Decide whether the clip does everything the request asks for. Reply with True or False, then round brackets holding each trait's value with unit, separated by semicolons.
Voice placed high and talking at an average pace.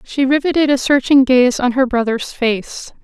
True (260 Hz; 180 wpm)